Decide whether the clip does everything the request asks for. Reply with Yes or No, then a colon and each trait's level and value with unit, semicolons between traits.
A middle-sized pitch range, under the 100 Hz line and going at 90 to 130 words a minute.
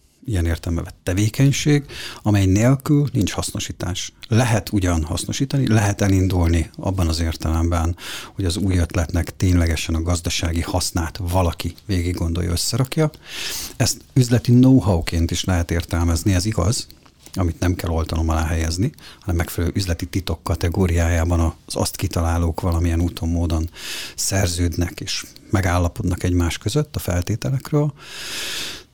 Yes: average, 3.7 semitones; very low, 90 Hz; average, 125 wpm